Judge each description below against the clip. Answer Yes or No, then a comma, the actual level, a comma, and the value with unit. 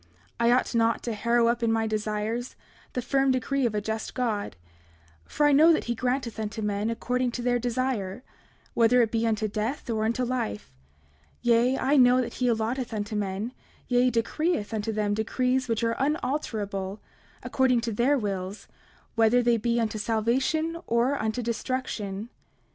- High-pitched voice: Yes, high, 235 Hz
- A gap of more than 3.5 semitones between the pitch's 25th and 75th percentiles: No, average, 2.7 semitones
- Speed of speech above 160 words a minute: Yes, average, 170 wpm